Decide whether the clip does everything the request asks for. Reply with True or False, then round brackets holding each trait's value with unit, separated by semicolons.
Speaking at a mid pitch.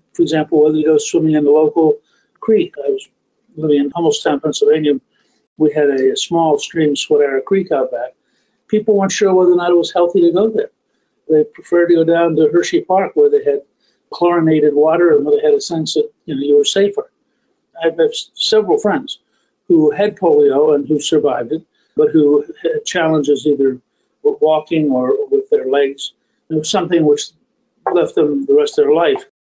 True (170 Hz)